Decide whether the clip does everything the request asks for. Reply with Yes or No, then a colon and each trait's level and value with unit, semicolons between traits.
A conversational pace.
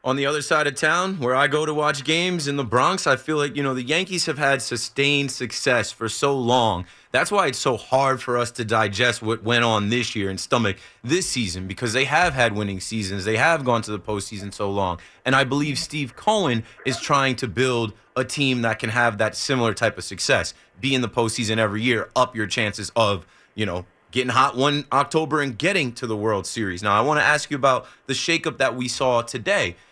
No: fast, 230 wpm